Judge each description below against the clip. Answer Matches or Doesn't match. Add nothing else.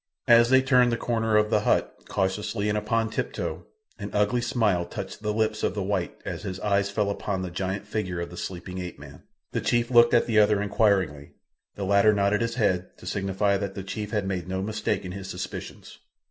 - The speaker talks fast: Matches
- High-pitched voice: Doesn't match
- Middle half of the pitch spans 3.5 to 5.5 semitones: Doesn't match